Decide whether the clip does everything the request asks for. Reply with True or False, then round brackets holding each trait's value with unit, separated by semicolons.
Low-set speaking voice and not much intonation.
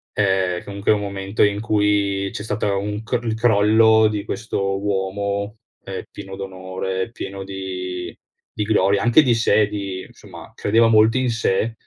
True (100 Hz; 2.2 semitones)